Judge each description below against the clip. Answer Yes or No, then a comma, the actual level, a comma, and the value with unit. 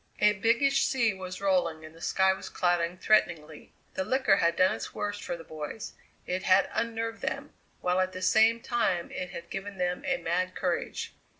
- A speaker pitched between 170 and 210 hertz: Yes, medium, 185 Hz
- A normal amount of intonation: Yes, average, 3.8 semitones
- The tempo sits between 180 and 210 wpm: Yes, average, 190 wpm